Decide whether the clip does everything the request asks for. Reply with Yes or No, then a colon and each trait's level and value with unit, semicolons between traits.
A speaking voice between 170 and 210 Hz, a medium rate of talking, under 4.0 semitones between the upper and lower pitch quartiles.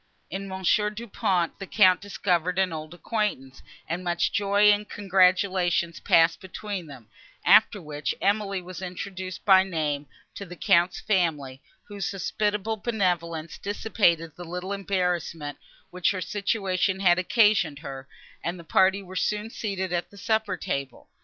Yes: medium, 185 Hz; average, 145 wpm; average, 2.9 semitones